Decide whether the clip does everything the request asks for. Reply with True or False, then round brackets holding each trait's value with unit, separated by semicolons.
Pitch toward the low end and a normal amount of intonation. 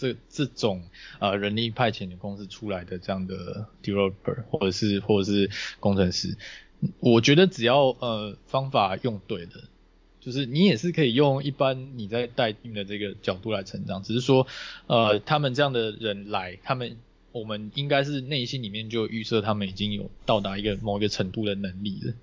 True (110 Hz; 4.3 semitones)